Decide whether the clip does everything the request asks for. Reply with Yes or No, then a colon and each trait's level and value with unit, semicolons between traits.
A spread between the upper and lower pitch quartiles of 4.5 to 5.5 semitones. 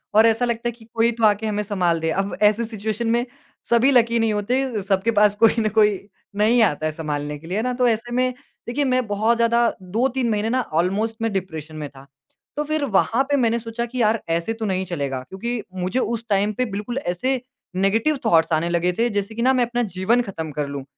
No: average, 4.0 semitones